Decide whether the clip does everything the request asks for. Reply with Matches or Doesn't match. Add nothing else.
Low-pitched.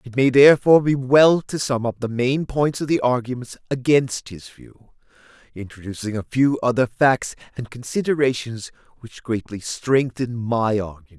Matches